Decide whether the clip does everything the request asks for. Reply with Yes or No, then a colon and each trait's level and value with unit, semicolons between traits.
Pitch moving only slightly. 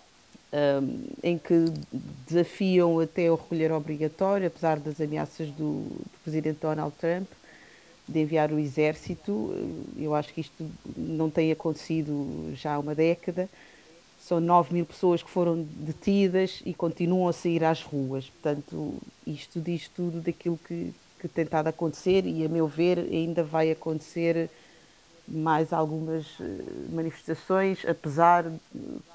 Yes: narrow, 1.7 semitones